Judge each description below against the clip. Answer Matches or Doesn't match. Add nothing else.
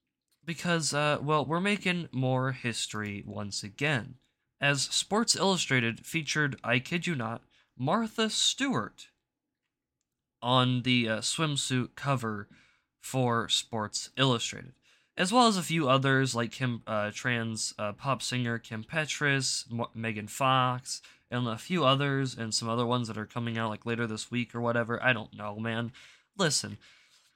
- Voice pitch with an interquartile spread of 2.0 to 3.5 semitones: Doesn't match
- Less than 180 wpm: Matches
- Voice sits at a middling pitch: Doesn't match